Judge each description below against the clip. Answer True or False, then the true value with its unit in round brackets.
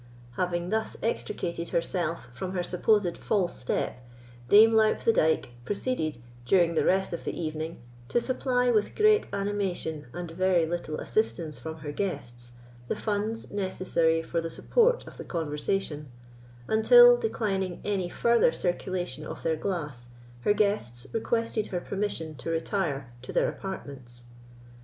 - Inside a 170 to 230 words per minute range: False (145 wpm)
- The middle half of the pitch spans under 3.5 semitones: False (4.7 semitones)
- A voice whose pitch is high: False (180 Hz)